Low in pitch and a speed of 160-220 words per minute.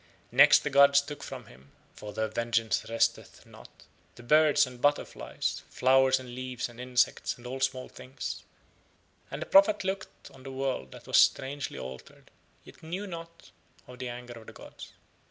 Yes: low, 130 Hz; average, 170 wpm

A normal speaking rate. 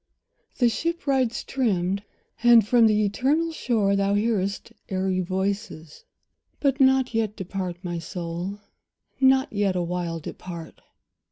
No: slow, 120 wpm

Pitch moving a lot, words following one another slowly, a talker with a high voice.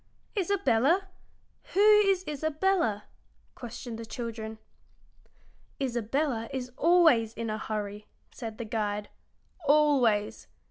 Yes: wide, 6.0 semitones; slow, 95 wpm; high, 245 Hz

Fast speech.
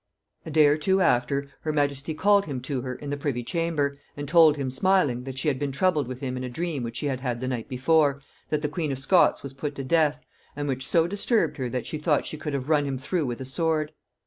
Yes: fast, 260 wpm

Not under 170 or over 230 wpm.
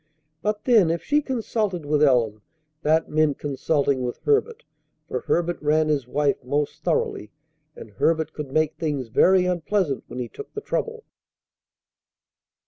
No: average, 145 wpm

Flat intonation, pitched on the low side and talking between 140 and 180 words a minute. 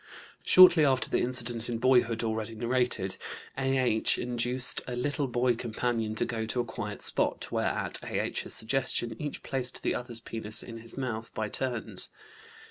Yes: narrow, 2.2 semitones; low, 120 Hz; average, 160 wpm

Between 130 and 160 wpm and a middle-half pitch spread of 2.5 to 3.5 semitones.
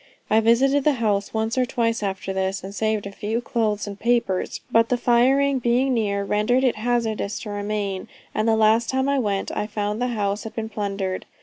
No: fast, 205 wpm; average, 2.8 semitones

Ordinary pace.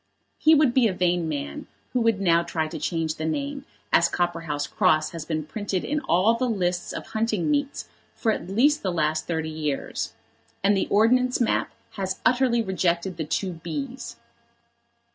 Yes: average, 175 wpm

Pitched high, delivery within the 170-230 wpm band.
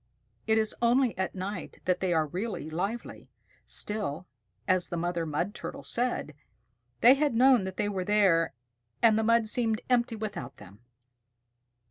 No: high, 205 Hz; average, 155 wpm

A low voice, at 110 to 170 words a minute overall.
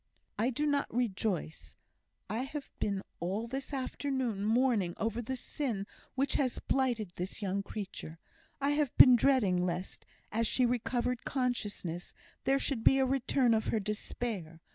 No: high, 235 Hz; average, 150 wpm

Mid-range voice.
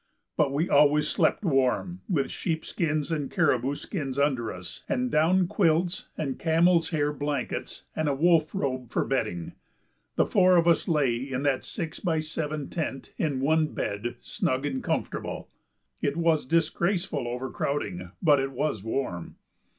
Yes: medium, 150 Hz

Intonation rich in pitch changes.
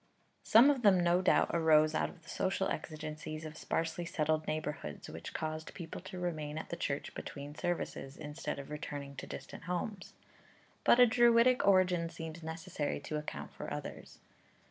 No: average, 3.1 semitones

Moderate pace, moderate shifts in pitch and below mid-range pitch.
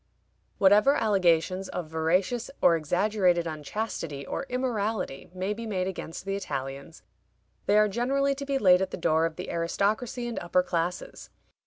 No: average, 155 wpm; average, 4.7 semitones; high, 190 Hz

